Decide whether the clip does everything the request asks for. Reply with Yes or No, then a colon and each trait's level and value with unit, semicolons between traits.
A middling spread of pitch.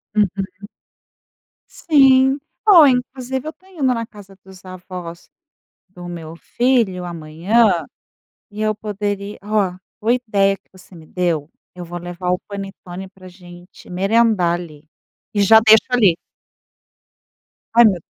Yes: average, 4.4 semitones